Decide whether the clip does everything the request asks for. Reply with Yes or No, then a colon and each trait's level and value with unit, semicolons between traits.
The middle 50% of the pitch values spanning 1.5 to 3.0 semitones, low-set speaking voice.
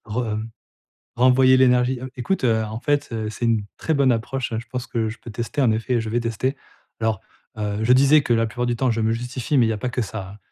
Yes: narrow, 2.6 semitones; low, 120 Hz